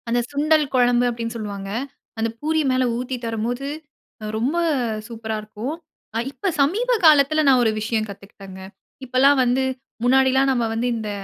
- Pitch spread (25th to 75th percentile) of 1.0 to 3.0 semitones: No, average, 3.7 semitones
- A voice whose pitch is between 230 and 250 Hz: Yes, high, 245 Hz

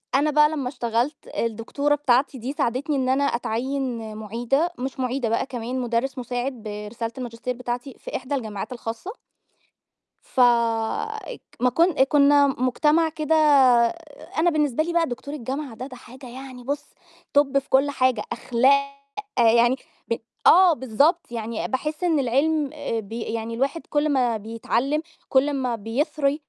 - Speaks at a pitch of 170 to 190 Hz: No, very high, 260 Hz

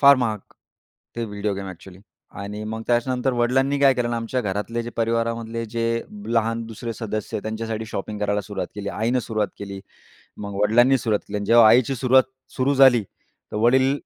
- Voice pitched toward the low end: Yes, low, 115 Hz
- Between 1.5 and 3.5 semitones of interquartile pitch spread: Yes, average, 2.8 semitones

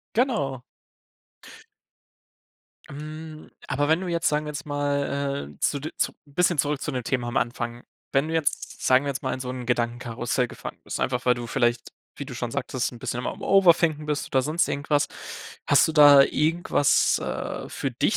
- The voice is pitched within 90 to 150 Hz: Yes, medium, 140 Hz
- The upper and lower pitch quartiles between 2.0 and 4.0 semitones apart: Yes, average, 3.4 semitones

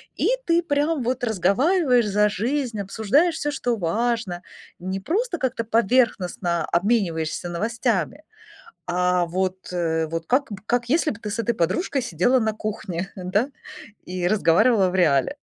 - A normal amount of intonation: No, wide, 5.7 semitones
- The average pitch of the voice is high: Yes, high, 215 Hz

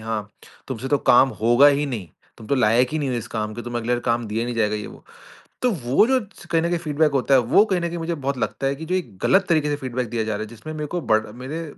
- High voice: No, low, 130 Hz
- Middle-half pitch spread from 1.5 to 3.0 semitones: No, average, 5.1 semitones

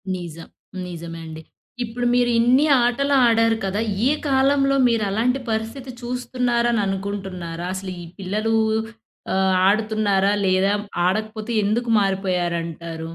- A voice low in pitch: No, high, 210 Hz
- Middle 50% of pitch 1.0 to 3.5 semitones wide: No, average, 4.2 semitones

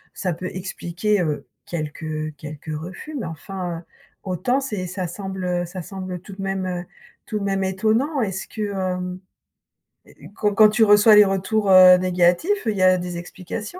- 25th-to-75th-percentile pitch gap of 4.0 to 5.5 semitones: No, average, 2.8 semitones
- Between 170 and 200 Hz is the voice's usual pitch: Yes, medium, 185 Hz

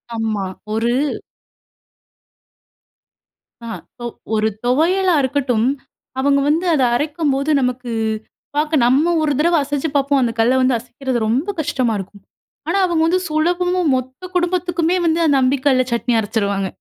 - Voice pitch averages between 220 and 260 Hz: No, very high, 280 Hz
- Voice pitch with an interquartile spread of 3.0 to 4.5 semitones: No, average, 4.9 semitones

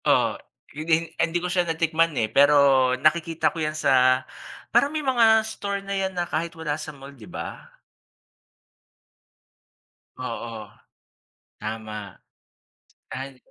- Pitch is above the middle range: No, medium, 160 Hz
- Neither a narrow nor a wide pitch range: No, wide, 5.8 semitones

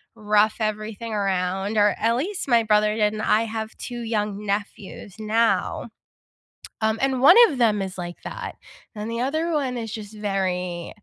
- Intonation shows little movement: Yes, narrow, 2.1 semitones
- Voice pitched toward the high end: Yes, high, 215 Hz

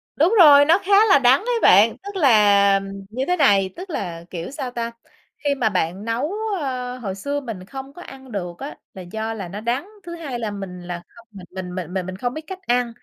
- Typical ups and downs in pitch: No, wide, 6.5 semitones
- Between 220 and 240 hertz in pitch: Yes, high, 235 Hz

